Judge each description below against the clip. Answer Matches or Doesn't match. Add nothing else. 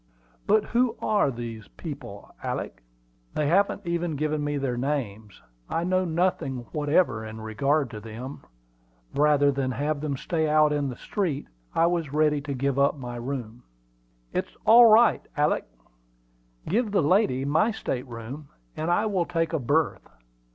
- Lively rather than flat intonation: Doesn't match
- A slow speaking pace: Doesn't match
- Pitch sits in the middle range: Matches